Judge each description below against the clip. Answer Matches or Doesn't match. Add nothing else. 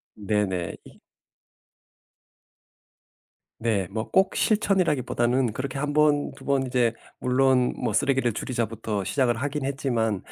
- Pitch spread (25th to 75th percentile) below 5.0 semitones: Matches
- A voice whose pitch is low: Matches